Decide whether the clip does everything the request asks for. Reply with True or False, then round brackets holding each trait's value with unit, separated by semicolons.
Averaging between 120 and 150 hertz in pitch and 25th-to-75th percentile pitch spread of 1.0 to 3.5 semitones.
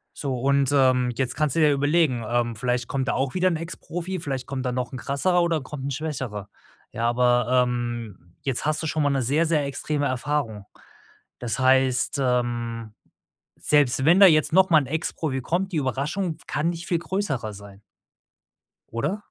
False (135 Hz; 4.1 semitones)